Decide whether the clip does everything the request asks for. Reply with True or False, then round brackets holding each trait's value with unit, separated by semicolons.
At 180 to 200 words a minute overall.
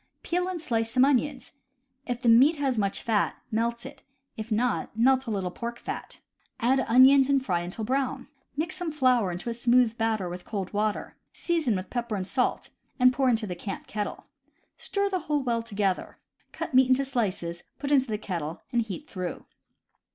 True (190 wpm)